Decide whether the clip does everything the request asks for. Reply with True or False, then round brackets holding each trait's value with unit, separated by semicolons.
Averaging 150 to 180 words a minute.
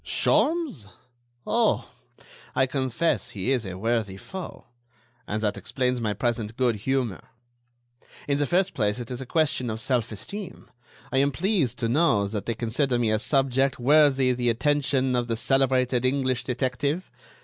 True (160 wpm)